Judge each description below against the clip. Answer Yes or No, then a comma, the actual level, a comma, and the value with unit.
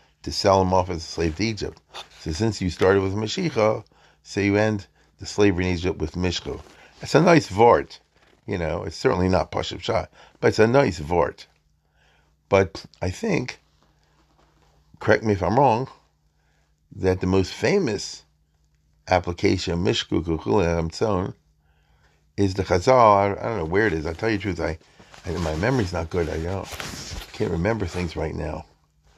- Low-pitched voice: Yes, very low, 90 Hz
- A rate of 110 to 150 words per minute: No, average, 170 wpm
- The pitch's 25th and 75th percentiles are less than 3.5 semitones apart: No, average, 4.4 semitones